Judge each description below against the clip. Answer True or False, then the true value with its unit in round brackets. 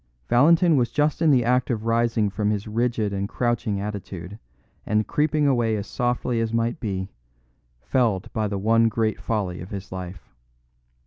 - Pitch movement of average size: True (3.3 semitones)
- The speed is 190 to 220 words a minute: False (175 wpm)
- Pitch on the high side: False (115 Hz)